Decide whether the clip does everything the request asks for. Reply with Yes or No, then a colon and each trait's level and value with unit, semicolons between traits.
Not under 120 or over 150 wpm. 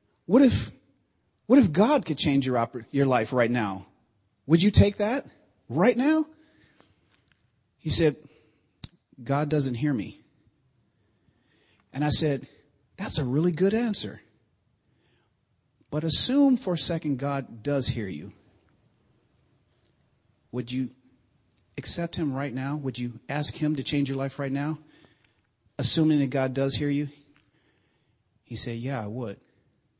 Yes: slow, 135 wpm